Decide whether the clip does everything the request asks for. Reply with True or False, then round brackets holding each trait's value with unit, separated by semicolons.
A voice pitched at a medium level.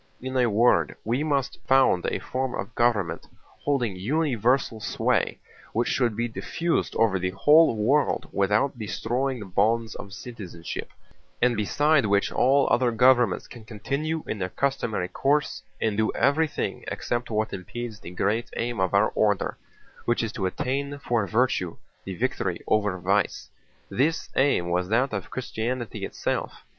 False (115 Hz)